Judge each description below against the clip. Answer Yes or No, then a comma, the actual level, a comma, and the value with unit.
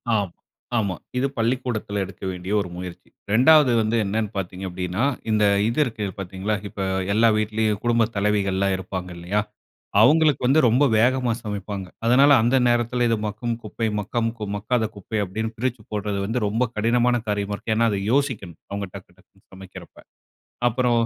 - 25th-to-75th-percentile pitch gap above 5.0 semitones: No, average, 3.3 semitones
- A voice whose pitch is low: Yes, low, 110 Hz